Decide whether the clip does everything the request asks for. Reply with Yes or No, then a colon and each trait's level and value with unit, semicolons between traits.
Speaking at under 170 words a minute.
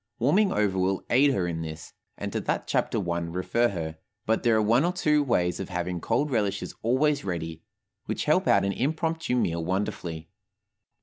No: average, 185 wpm